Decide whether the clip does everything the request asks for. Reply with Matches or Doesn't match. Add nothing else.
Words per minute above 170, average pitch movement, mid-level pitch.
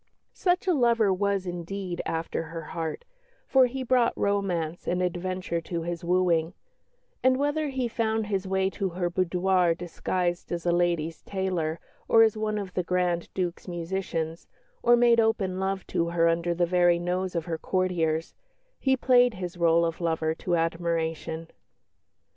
Doesn't match